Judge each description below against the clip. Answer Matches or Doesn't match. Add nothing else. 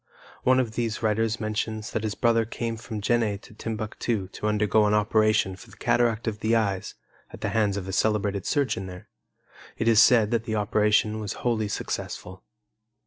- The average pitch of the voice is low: Matches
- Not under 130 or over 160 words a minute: Doesn't match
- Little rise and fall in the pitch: Matches